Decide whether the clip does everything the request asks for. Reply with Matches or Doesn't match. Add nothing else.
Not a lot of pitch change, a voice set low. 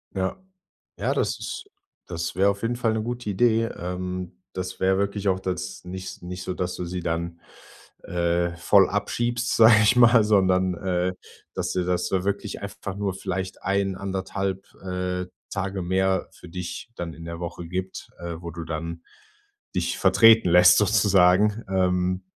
Matches